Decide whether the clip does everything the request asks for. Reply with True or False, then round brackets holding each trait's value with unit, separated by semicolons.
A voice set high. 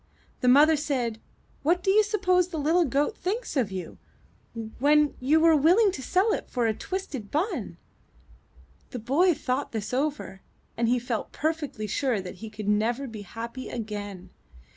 True (275 Hz)